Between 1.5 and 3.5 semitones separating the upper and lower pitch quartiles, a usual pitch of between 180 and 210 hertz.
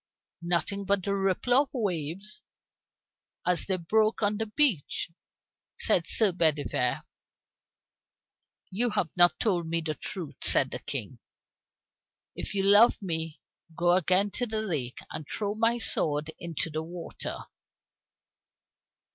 No: average, 4.4 semitones; medium, 185 Hz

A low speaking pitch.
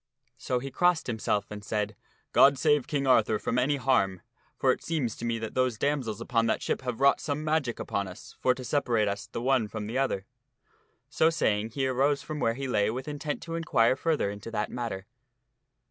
Yes: low, 125 Hz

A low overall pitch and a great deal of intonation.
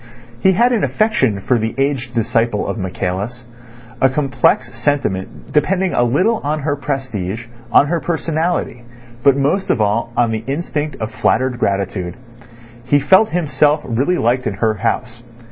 No: low, 130 Hz; average, 5.0 semitones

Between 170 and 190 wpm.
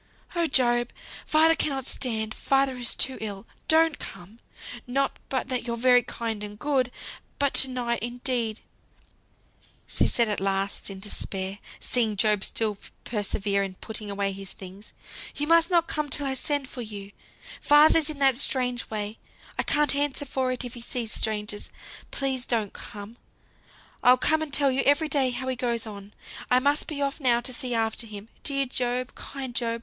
Yes: average, 180 wpm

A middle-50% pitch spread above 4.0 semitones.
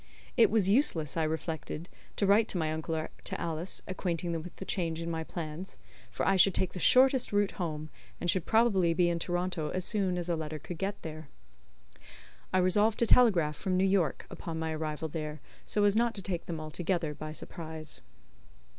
No: average, 3.3 semitones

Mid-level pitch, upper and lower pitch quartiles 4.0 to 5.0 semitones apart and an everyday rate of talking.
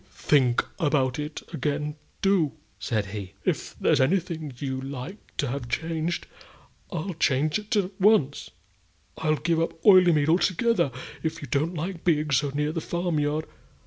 No: medium, 155 Hz; average, 3.6 semitones; average, 155 wpm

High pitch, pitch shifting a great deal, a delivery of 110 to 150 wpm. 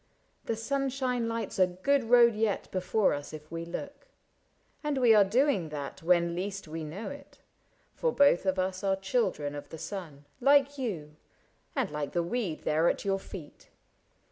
No: high, 195 Hz; wide, 6.6 semitones; average, 170 wpm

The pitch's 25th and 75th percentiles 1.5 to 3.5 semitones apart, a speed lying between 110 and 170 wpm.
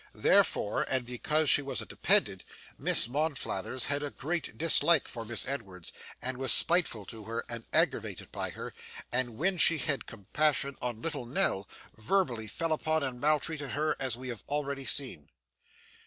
No: average, 4.6 semitones; average, 165 wpm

